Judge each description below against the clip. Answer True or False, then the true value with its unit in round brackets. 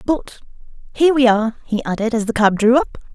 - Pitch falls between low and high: False (235 Hz)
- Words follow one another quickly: True (210 wpm)